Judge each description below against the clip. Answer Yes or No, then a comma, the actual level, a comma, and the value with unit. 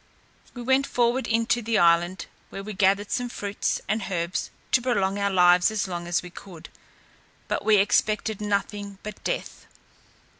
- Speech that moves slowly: No, average, 160 wpm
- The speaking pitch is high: Yes, high, 205 Hz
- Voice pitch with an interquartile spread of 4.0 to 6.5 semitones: No, average, 3.3 semitones